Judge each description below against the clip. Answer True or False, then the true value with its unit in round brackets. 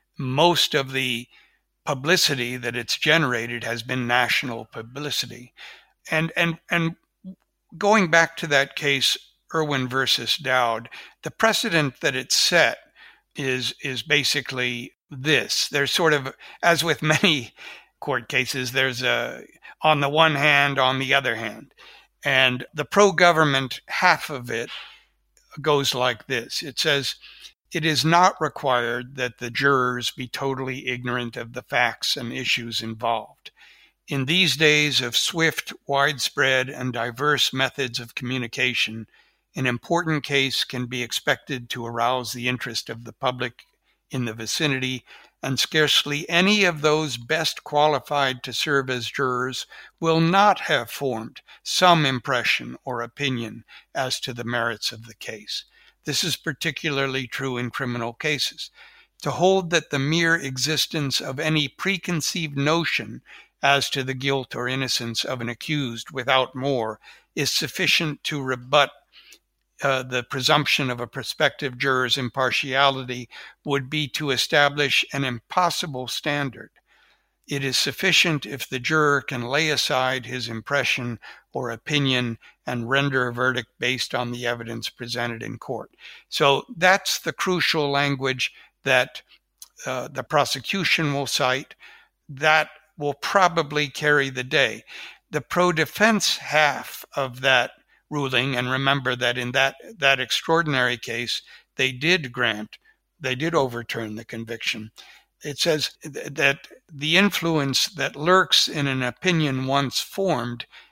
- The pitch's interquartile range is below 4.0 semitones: True (3.6 semitones)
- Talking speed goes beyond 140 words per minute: False (135 wpm)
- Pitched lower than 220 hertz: True (135 Hz)